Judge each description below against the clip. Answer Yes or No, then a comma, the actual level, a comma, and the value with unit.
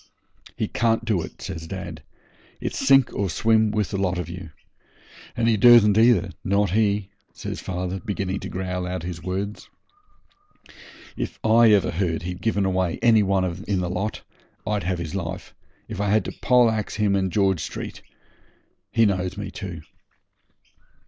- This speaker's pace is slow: No, average, 165 wpm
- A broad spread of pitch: No, average, 2.8 semitones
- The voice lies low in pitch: Yes, very low, 95 Hz